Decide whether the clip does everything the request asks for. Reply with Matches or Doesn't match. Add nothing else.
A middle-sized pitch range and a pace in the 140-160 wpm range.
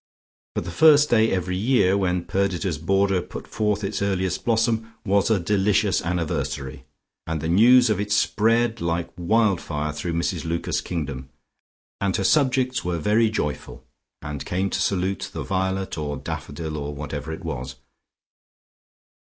Matches